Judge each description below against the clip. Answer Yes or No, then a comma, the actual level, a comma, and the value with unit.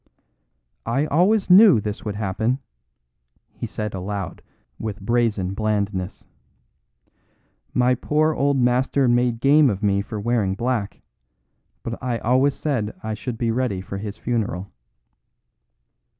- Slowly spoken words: Yes, slow, 125 wpm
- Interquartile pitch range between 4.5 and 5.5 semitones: No, average, 3.9 semitones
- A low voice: Yes, low, 115 Hz